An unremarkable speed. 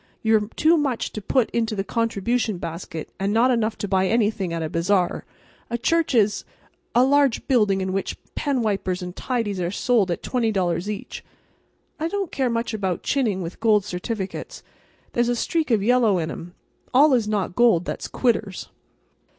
Yes: average, 170 wpm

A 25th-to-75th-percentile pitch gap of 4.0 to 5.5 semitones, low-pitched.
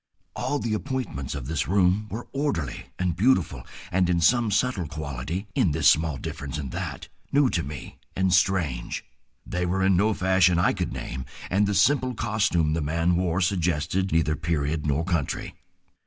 Yes: average, 4.3 semitones; very low, 90 Hz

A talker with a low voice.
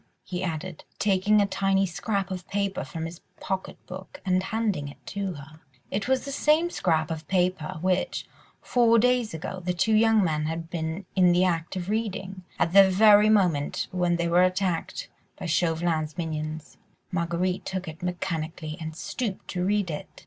No: medium, 185 Hz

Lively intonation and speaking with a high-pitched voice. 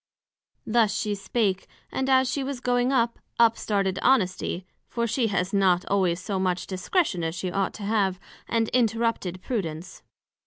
No: average, 4.1 semitones; high, 205 Hz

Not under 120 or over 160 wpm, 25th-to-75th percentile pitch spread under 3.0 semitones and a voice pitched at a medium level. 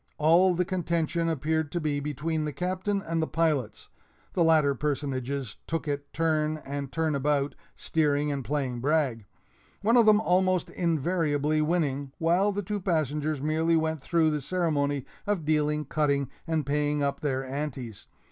Yes: average, 155 wpm; narrow, 2.6 semitones; medium, 155 Hz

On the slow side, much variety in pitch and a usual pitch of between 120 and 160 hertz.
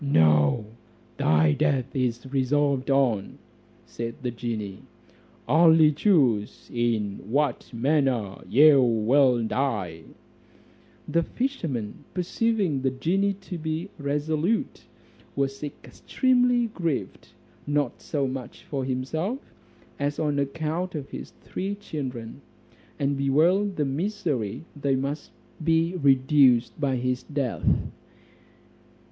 No: slow, 105 wpm; average, 4.5 semitones; medium, 140 Hz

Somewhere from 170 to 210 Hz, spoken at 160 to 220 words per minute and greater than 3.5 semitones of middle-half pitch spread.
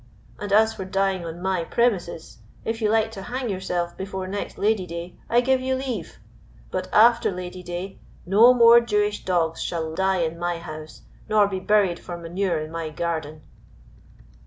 Yes: high, 190 Hz; average, 175 wpm; average, 4.0 semitones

